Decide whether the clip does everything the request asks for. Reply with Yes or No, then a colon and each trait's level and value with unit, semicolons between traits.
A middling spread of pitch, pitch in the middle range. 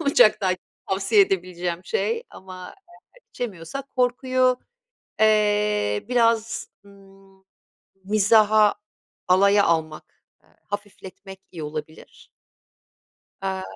No: average, 3.4 semitones; high, 200 Hz